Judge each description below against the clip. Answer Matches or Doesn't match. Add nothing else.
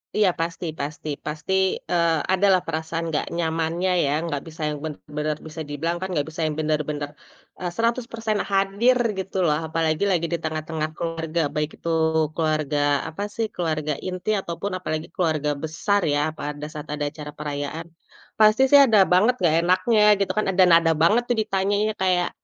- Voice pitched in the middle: Matches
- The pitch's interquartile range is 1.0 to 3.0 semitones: Doesn't match